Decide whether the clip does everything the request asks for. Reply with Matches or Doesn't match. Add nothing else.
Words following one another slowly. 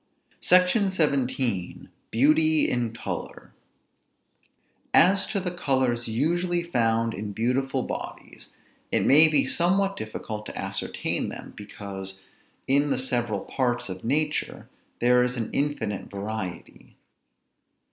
Matches